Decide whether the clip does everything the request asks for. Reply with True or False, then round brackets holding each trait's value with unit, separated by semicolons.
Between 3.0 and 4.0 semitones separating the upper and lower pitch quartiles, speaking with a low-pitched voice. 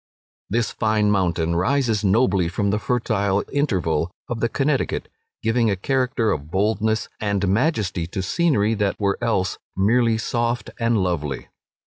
True (3.7 semitones; 105 Hz)